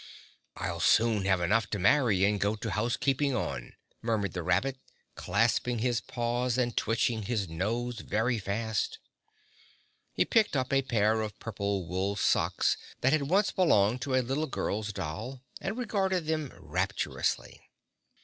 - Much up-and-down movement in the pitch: No, average, 4.3 semitones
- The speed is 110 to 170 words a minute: Yes, average, 150 wpm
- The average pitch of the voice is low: Yes, low, 115 Hz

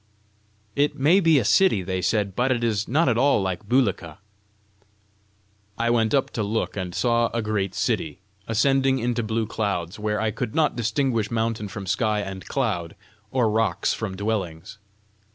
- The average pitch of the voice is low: Yes, low, 110 Hz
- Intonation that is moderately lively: Yes, average, 3.4 semitones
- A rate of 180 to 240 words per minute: No, average, 170 wpm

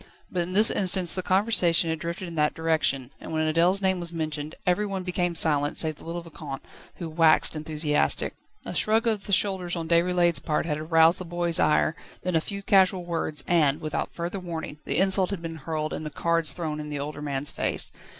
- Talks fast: Yes, fast, 210 wpm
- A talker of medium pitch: Yes, medium, 170 Hz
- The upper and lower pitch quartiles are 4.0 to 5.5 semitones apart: No, average, 2.8 semitones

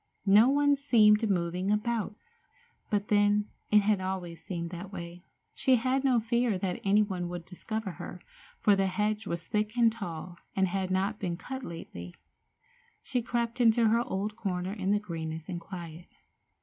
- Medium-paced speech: Yes, average, 170 wpm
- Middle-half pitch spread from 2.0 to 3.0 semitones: No, average, 3.8 semitones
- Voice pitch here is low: No, high, 200 Hz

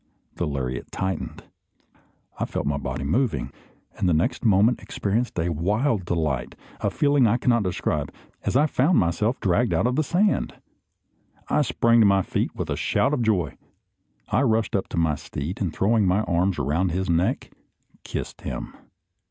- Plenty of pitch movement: Yes, wide, 6.0 semitones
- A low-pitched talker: Yes, very low, 95 Hz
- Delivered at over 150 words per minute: Yes, average, 170 wpm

